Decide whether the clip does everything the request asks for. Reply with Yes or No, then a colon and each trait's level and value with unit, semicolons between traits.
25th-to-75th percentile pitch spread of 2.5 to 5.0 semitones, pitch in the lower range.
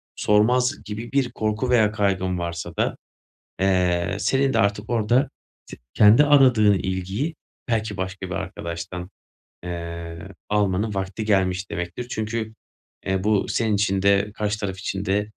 Yes: average, 2.9 semitones; low, 105 Hz